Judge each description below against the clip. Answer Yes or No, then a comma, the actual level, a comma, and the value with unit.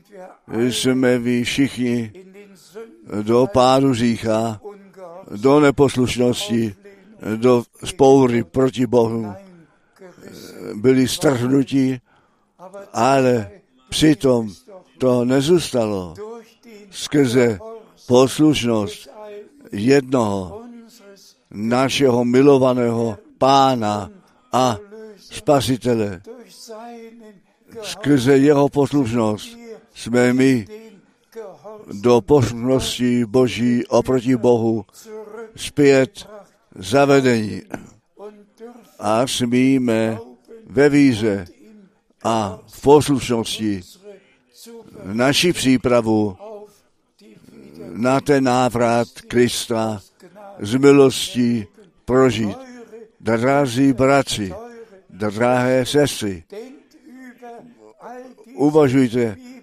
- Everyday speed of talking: No, slow, 60 wpm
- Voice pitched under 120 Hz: No, low, 135 Hz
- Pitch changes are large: Yes, wide, 8.4 semitones